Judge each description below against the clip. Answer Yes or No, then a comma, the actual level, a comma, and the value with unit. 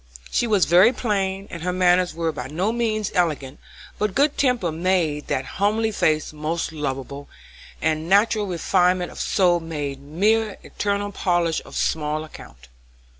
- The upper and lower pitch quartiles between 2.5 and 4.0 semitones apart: No, average, 4.6 semitones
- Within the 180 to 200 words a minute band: No, average, 150 wpm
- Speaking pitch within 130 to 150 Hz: No, medium, 180 Hz